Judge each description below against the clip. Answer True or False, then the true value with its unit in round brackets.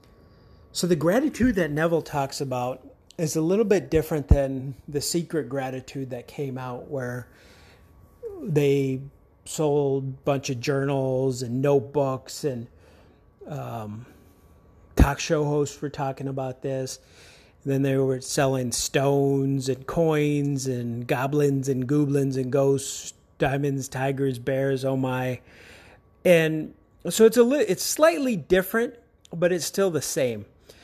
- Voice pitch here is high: False (140 Hz)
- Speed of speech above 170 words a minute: False (135 wpm)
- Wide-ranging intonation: False (3.1 semitones)